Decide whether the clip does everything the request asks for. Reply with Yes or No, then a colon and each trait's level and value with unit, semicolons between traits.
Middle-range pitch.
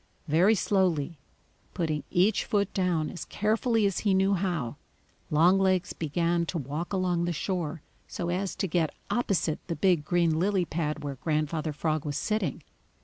Yes: medium, 175 Hz